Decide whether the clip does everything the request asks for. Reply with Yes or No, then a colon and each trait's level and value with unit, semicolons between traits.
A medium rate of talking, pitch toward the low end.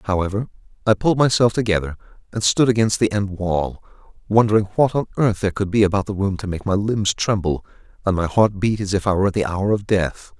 No: fast, 225 wpm; low, 100 Hz